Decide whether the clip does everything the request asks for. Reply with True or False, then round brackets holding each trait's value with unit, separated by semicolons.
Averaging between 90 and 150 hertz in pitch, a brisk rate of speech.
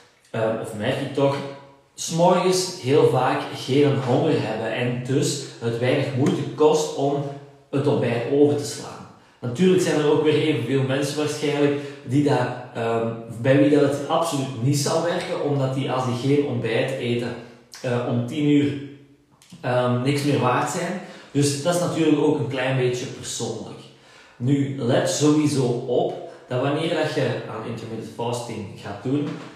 False (140 Hz; 160 wpm)